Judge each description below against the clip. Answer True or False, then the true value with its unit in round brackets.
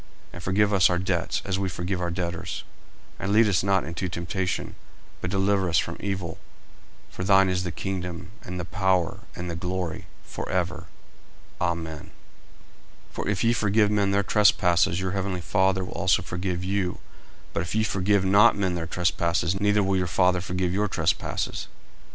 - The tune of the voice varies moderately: False (2.0 semitones)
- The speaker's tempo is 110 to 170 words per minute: False (185 wpm)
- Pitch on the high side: False (95 Hz)